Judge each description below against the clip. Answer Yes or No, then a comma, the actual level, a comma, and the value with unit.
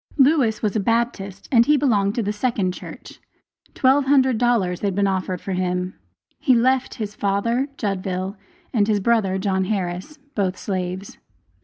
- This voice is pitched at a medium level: No, high, 205 Hz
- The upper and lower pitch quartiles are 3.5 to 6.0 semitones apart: Yes, average, 4.0 semitones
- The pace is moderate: Yes, average, 155 wpm